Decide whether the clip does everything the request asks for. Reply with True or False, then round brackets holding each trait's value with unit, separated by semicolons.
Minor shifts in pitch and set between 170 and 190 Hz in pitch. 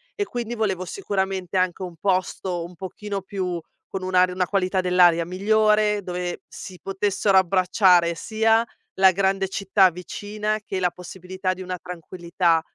True (1.8 semitones; 185 Hz)